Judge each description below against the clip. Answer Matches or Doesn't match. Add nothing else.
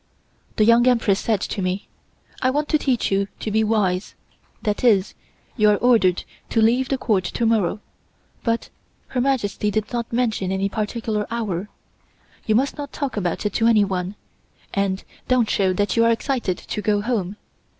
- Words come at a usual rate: Matches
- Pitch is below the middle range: Doesn't match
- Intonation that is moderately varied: Matches